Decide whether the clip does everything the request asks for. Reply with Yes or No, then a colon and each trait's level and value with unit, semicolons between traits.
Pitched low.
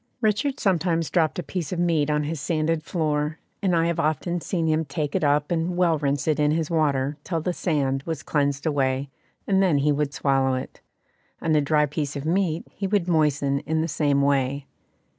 No: medium, 155 Hz